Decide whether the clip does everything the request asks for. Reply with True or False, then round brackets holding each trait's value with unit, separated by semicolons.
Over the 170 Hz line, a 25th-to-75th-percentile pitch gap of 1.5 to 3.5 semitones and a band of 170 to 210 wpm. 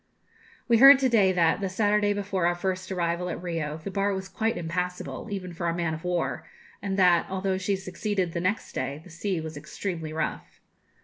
True (185 Hz; 2.8 semitones; 200 wpm)